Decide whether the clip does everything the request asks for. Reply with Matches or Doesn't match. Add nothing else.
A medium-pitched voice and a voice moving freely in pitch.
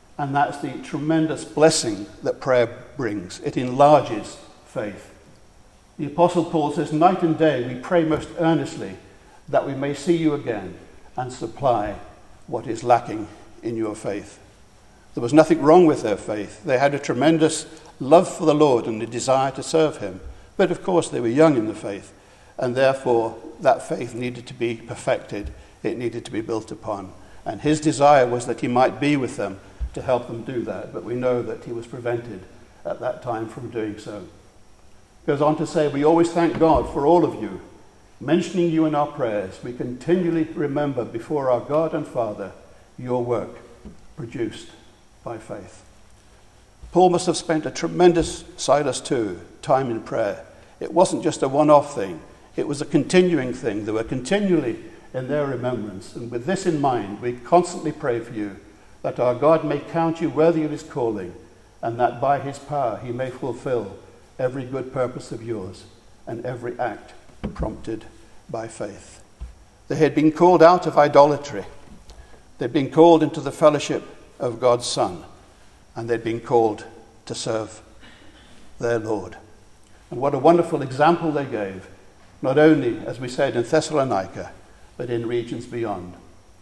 Doesn't match